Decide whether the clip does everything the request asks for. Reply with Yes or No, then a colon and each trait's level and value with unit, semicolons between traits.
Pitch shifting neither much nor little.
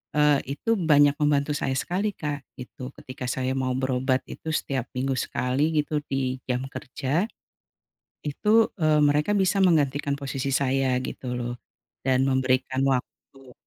No: narrow, 2.3 semitones